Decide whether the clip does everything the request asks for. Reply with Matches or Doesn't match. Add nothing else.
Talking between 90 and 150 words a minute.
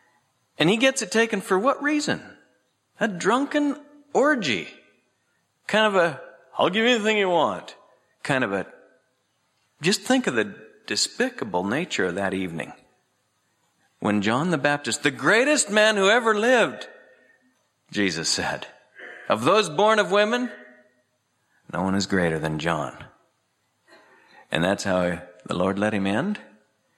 Matches